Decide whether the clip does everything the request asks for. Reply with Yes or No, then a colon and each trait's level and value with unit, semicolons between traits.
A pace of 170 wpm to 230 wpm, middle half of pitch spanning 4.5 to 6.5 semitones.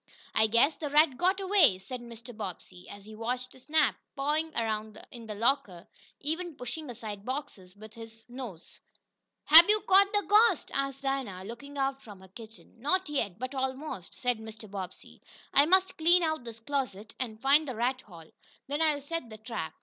Yes: average, 180 wpm; wide, 5.5 semitones